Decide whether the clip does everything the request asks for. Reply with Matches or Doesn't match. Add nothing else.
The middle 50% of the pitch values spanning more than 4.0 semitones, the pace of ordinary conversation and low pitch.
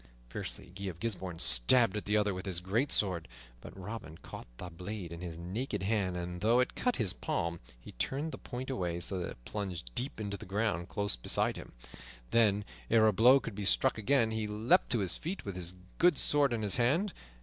Doesn't match